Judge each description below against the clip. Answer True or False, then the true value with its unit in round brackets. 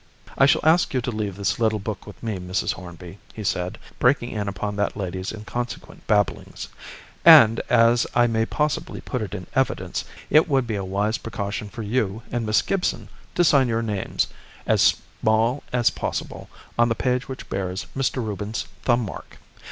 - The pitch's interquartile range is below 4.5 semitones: True (3.3 semitones)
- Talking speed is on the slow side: False (180 wpm)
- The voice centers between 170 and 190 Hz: False (110 Hz)